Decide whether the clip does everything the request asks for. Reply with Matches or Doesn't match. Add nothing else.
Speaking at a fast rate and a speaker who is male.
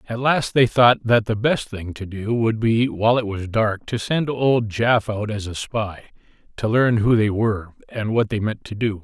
Matches